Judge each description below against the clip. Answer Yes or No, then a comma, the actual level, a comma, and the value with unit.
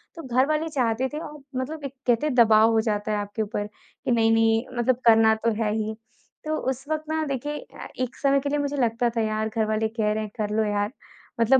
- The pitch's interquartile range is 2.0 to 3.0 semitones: No, average, 4.1 semitones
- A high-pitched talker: Yes, high, 230 Hz